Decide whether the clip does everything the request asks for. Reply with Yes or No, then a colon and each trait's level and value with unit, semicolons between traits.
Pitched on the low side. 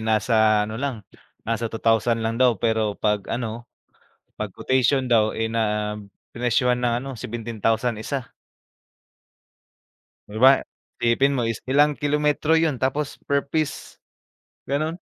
Yes: low, 120 Hz